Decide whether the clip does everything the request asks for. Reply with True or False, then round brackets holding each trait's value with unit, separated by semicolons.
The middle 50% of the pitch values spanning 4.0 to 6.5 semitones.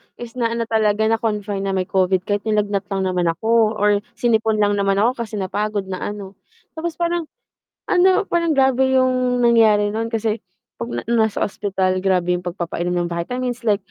False (3.5 semitones)